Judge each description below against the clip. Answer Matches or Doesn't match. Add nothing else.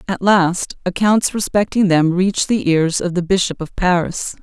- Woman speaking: Matches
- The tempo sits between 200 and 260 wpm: Doesn't match